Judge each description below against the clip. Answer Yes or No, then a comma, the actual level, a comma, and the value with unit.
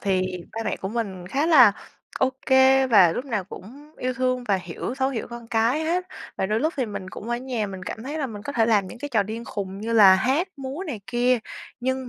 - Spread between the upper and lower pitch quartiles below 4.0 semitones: No, average, 4.3 semitones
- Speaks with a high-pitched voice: Yes, high, 240 Hz